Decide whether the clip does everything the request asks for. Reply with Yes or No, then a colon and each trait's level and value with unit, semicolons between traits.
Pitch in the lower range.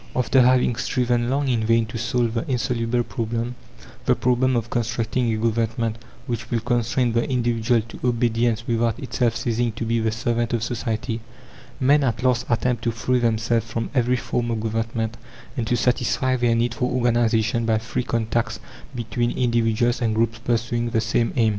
Yes: low, 115 Hz